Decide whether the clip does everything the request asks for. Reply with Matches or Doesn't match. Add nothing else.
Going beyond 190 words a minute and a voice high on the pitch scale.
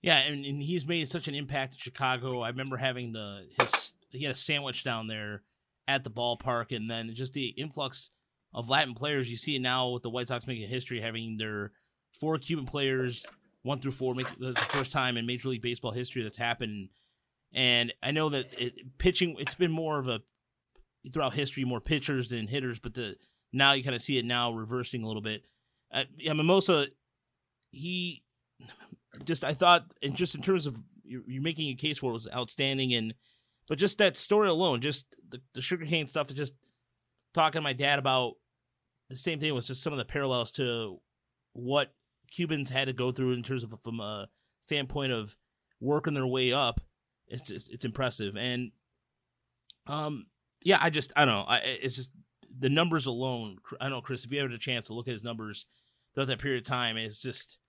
Doesn't match